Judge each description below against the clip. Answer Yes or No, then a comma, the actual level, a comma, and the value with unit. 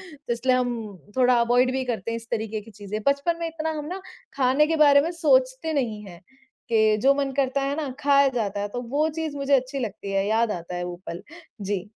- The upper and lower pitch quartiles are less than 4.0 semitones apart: No, average, 4.7 semitones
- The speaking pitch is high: Yes, very high, 255 Hz